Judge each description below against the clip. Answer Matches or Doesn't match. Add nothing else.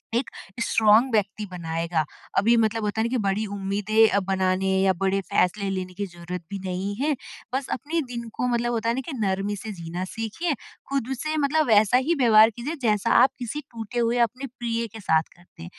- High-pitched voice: Matches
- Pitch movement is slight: Doesn't match